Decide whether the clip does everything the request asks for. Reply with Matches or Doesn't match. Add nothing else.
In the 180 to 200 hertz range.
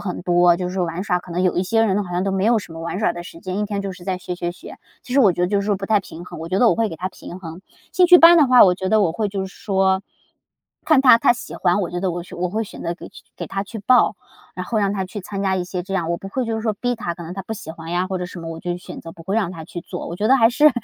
Matches